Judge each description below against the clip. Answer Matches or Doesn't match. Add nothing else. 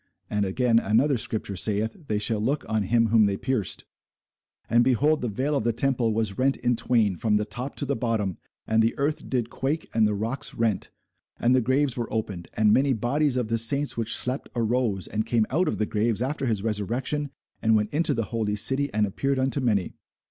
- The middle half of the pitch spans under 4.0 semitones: Matches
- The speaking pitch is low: Matches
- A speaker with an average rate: Doesn't match